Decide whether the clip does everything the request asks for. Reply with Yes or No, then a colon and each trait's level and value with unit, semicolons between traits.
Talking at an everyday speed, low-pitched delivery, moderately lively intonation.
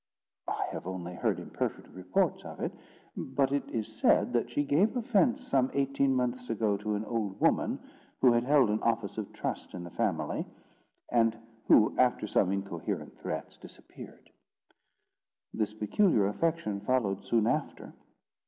Yes: average, 155 wpm; low, 115 Hz; average, 4.7 semitones